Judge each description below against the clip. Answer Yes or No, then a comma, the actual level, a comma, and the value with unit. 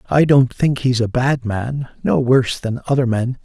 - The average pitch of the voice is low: Yes, low, 125 Hz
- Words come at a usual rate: Yes, average, 190 wpm